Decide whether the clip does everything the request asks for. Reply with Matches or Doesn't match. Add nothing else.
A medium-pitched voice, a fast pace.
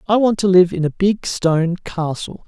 Matches